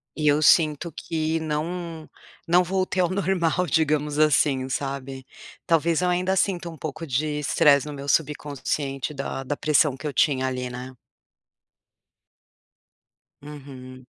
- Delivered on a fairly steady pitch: No, average, 3.2 semitones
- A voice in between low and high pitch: Yes, medium, 150 Hz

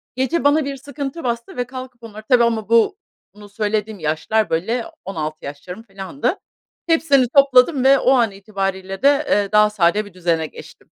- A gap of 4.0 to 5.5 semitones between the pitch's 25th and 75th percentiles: Yes, average, 5.1 semitones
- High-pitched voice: Yes, high, 220 Hz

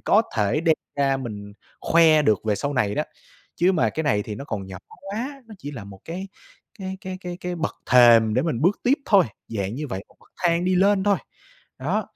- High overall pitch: No, medium, 150 Hz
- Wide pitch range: Yes, wide, 8.9 semitones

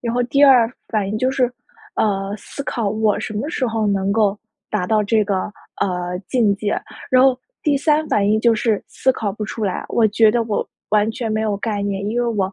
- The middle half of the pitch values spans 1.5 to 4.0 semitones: Yes, average, 2.8 semitones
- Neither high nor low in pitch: No, high, 215 Hz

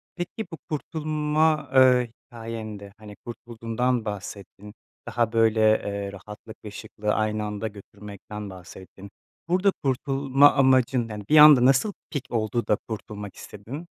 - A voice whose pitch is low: Yes, low, 115 Hz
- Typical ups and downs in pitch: Yes, average, 4.5 semitones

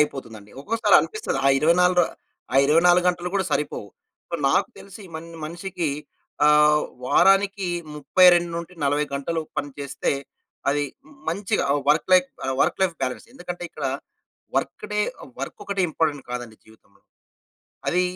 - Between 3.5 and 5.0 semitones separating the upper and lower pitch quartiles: Yes, average, 4.2 semitones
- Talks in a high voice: No, medium, 165 Hz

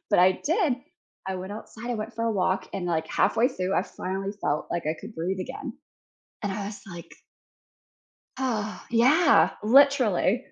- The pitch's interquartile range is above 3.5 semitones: Yes, average, 4.5 semitones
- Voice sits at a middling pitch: No, high, 210 Hz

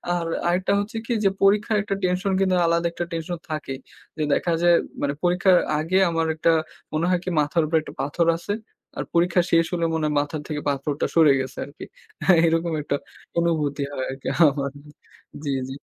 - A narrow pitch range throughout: No, average, 3.1 semitones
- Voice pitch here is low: No, medium, 165 Hz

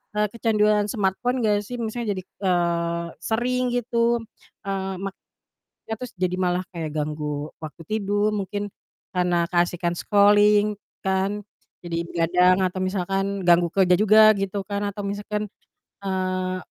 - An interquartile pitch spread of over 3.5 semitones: No, average, 2.8 semitones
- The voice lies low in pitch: No, high, 195 Hz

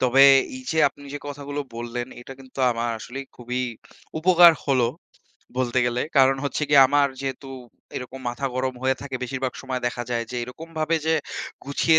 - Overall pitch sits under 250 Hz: Yes, low, 135 Hz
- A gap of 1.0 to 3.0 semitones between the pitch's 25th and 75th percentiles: Yes, narrow, 2.4 semitones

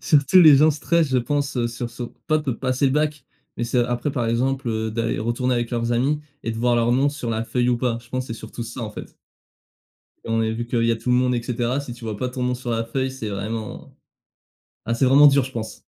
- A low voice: Yes, low, 125 Hz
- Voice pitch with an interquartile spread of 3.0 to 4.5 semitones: No, narrow, 2.5 semitones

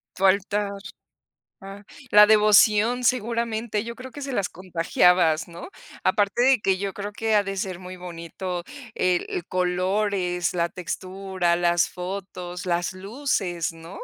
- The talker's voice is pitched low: No, high, 190 Hz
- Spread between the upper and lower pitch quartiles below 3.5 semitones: Yes, average, 2.8 semitones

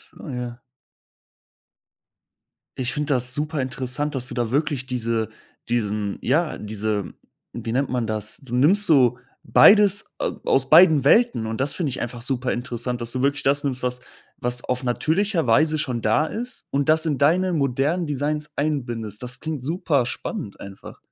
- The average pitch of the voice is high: No, low, 130 Hz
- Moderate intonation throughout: Yes, average, 4.1 semitones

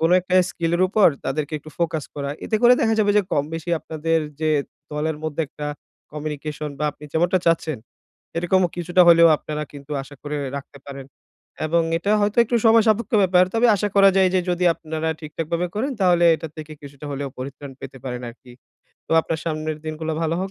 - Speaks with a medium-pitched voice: Yes, medium, 160 Hz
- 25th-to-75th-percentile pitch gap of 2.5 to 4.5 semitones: Yes, average, 3.3 semitones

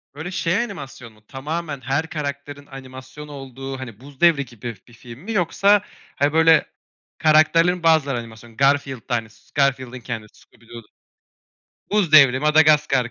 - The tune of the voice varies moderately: Yes, average, 3.7 semitones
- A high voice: No, medium, 140 Hz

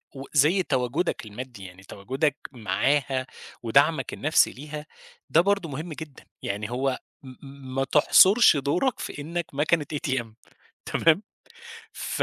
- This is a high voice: No, medium, 140 Hz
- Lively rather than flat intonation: No, average, 3.4 semitones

